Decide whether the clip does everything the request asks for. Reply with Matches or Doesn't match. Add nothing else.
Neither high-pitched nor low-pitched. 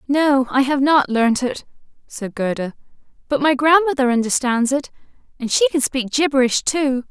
Doesn't match